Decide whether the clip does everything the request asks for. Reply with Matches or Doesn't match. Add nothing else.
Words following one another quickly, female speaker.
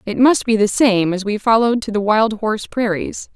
Matches